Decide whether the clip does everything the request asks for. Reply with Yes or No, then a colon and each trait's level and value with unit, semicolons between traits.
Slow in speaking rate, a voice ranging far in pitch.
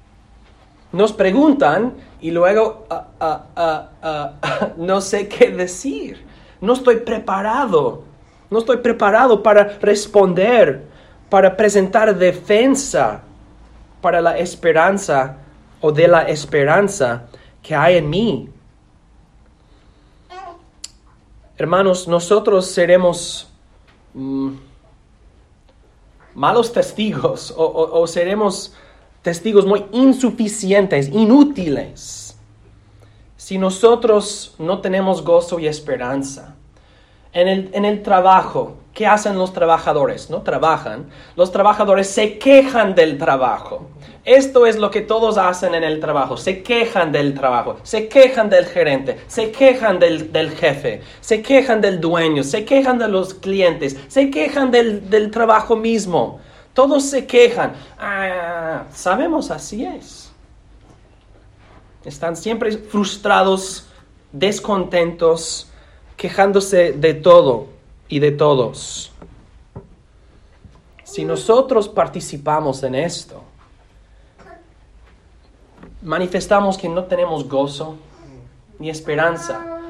Yes: slow, 105 wpm; wide, 6.4 semitones